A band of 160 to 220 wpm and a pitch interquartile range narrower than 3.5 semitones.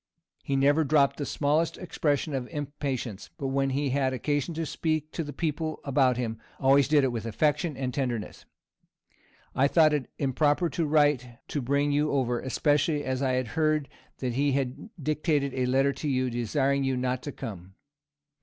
Yes: average, 175 wpm; narrow, 2.6 semitones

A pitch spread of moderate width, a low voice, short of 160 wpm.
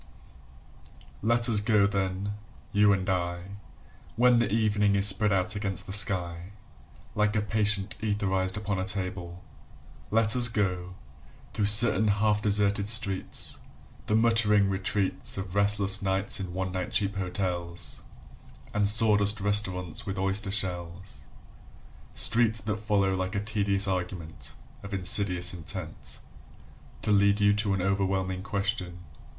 No: narrow, 2.0 semitones; low, 100 Hz; slow, 135 wpm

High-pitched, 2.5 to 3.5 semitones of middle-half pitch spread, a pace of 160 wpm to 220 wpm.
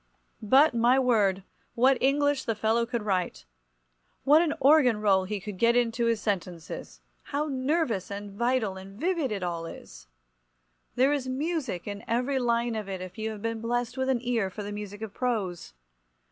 No: high, 230 Hz; average, 4.4 semitones; average, 180 wpm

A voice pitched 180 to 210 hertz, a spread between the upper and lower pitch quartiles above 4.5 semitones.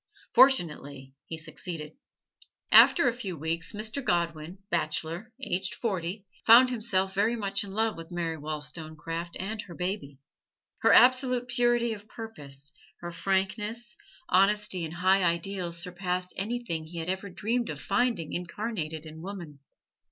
Yes: medium, 185 Hz; average, 5.0 semitones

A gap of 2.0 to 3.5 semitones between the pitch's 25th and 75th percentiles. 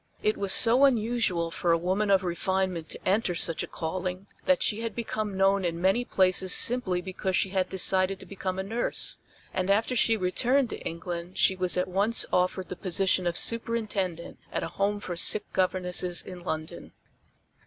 Yes: average, 2.7 semitones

